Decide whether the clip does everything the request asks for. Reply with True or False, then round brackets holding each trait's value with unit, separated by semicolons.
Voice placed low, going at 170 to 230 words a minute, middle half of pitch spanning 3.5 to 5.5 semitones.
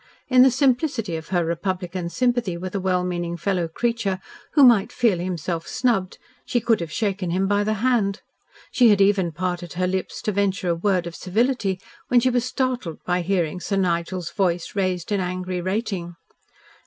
False (190 Hz; 180 wpm; 4.0 semitones)